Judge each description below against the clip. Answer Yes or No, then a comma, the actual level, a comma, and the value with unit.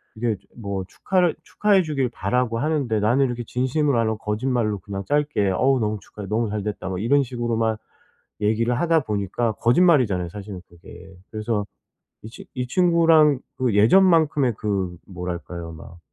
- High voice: No, low, 115 Hz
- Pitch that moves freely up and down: No, average, 5.0 semitones